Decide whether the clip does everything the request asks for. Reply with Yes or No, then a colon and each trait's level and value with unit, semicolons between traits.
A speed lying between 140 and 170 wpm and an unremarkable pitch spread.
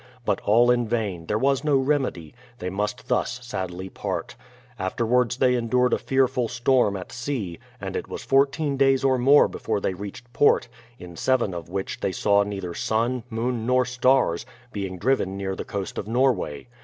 No: average, 180 wpm; average, 4.8 semitones